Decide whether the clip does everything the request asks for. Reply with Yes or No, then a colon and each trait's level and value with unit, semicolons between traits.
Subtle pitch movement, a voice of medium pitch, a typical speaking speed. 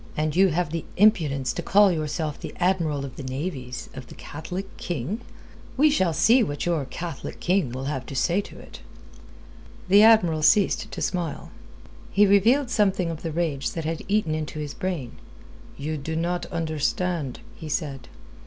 No: average, 4.4 semitones; medium, 165 Hz; average, 170 wpm